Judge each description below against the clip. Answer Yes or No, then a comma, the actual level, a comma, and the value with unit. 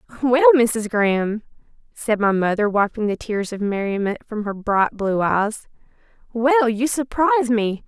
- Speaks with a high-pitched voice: Yes, high, 220 Hz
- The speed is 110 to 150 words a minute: Yes, average, 145 wpm